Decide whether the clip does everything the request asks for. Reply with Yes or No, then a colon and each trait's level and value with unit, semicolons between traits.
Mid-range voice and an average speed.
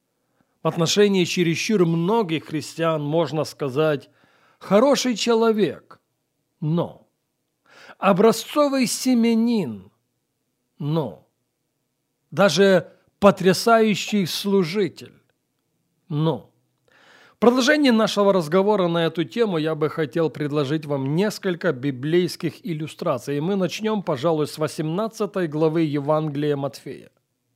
No: medium, 165 Hz; slow, 90 wpm